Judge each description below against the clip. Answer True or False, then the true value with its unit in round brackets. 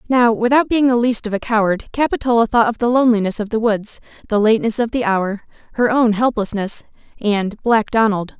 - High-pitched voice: True (225 Hz)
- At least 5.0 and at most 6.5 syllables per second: True (5.5 syllables/s)